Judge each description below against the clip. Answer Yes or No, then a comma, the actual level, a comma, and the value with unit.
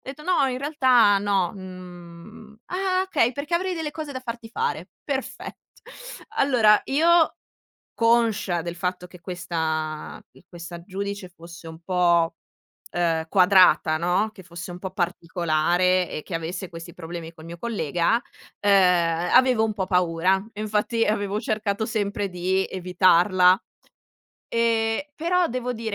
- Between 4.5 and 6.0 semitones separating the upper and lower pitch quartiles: Yes, average, 4.9 semitones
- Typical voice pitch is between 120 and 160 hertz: No, high, 190 Hz